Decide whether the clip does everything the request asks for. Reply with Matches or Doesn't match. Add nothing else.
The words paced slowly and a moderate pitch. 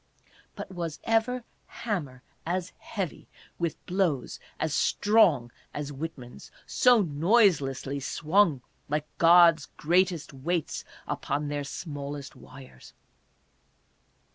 Matches